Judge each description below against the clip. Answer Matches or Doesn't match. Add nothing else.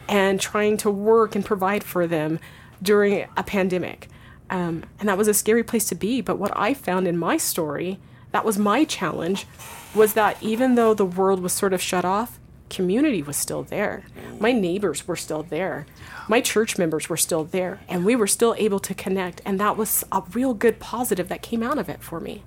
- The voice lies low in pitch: Doesn't match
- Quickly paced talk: Matches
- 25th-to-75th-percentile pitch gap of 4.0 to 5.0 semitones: Doesn't match